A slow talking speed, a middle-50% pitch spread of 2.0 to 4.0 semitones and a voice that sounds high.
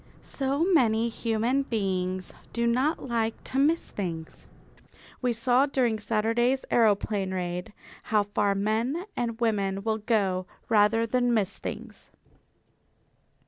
Yes: slow, 120 wpm; average, 3.3 semitones; high, 225 Hz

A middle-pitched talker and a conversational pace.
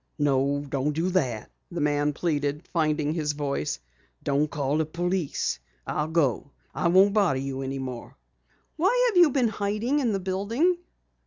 Yes: medium, 155 Hz; average, 160 wpm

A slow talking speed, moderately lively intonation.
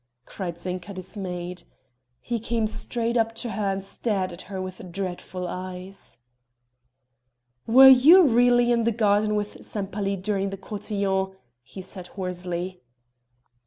Yes: slow, 130 wpm; average, 3.3 semitones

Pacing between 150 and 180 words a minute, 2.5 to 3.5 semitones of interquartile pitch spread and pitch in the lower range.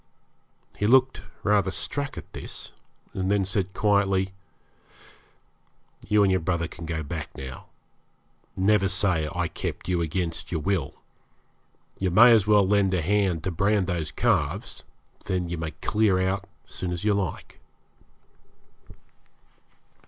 No: average, 140 wpm; average, 2.9 semitones; very low, 95 Hz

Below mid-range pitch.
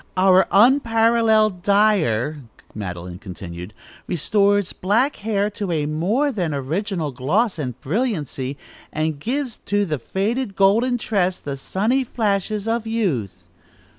No: high, 195 Hz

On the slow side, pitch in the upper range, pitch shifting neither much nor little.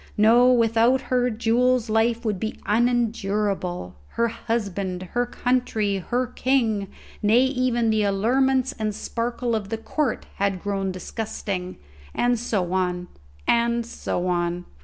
Yes: slow, 130 wpm; high, 225 Hz; average, 3.6 semitones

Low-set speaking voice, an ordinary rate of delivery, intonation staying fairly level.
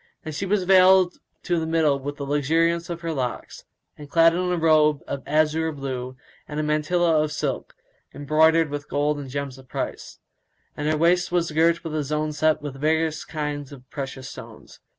No: medium, 155 Hz; average, 190 wpm; narrow, 2.3 semitones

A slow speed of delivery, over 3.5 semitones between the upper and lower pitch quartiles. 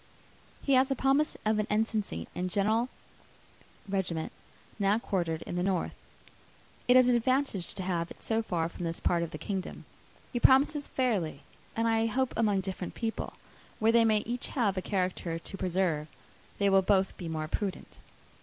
No: average, 180 wpm; average, 4.3 semitones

